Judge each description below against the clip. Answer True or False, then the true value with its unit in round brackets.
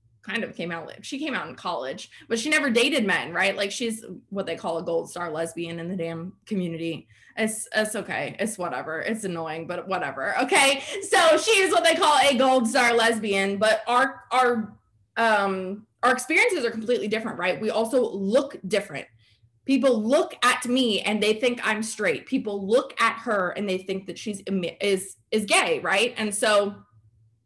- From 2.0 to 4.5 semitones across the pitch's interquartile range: False (5.3 semitones)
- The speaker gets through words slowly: False (190 wpm)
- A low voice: False (215 Hz)